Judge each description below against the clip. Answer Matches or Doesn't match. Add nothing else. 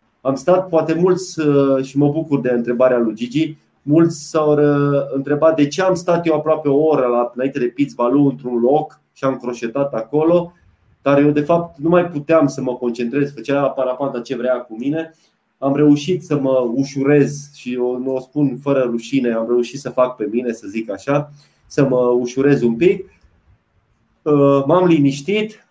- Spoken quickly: Matches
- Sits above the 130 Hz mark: Matches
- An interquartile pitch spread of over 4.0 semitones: Doesn't match